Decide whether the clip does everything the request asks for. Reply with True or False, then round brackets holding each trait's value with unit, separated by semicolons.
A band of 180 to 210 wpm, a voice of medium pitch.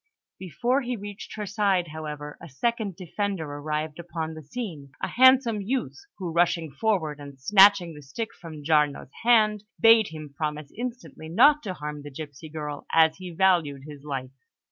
False (165 wpm; 165 Hz)